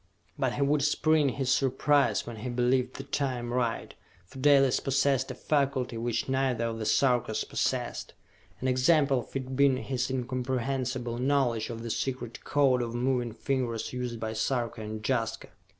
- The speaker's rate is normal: Yes, average, 165 wpm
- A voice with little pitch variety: Yes, narrow, 2.3 semitones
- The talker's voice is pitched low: Yes, low, 130 Hz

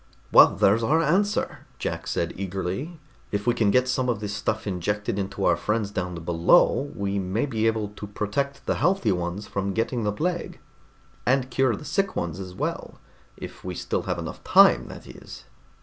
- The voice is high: No, low, 105 Hz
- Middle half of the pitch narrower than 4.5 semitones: No, average, 4.9 semitones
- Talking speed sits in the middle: Yes, average, 185 wpm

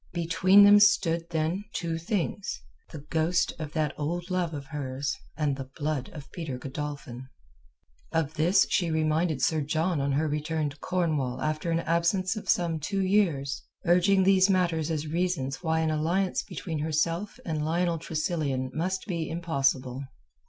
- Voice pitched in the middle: Yes, medium, 160 Hz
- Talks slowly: No, average, 160 wpm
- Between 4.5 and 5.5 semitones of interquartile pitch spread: No, average, 3.0 semitones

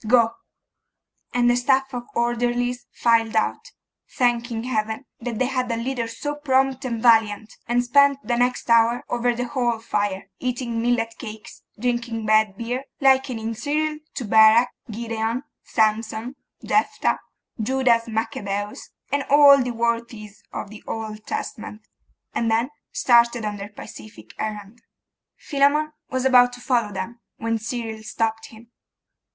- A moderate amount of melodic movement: No, narrow, 2.1 semitones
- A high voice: Yes, high, 235 Hz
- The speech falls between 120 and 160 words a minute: Yes, average, 140 wpm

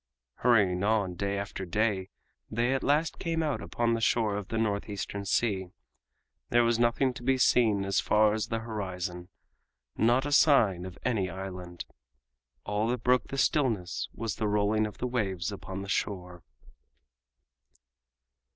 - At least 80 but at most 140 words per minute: No, average, 155 wpm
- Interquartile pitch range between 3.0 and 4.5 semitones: Yes, average, 3.6 semitones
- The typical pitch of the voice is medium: No, low, 105 Hz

